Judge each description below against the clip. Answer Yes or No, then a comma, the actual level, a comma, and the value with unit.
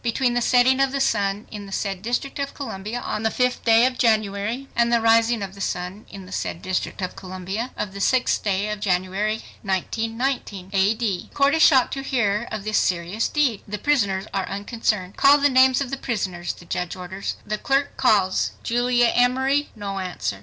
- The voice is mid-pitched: No, high, 215 Hz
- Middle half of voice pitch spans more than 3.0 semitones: Yes, average, 4.3 semitones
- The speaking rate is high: Yes, fast, 210 wpm